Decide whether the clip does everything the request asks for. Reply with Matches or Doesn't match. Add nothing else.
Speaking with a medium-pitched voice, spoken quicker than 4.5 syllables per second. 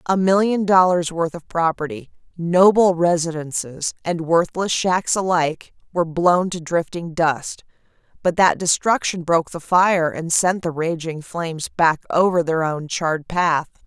Doesn't match